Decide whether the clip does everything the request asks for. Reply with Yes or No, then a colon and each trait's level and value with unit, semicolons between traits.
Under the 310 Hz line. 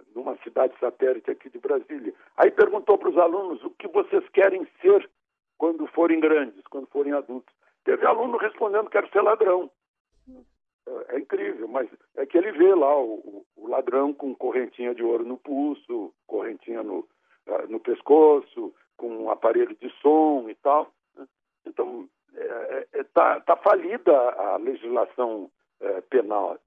No: very high, 350 Hz